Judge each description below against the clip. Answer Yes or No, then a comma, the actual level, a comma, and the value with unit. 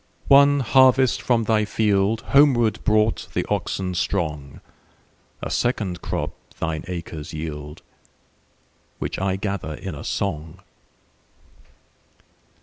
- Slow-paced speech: Yes, slow, 90 wpm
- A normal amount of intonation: No, wide, 5.8 semitones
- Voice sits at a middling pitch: No, low, 100 Hz